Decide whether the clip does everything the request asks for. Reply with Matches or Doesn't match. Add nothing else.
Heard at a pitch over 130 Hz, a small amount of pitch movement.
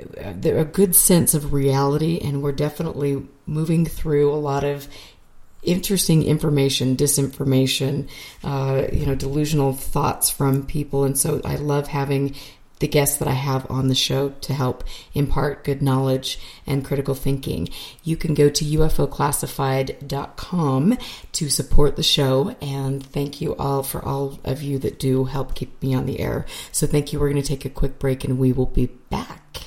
Matches